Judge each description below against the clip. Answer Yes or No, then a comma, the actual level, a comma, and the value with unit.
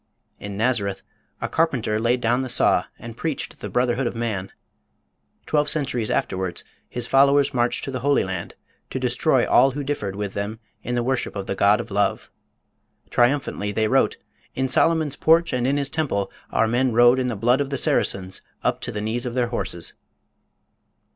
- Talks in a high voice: No, low, 120 Hz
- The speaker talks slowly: No, average, 185 wpm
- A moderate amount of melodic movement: Yes, average, 4.3 semitones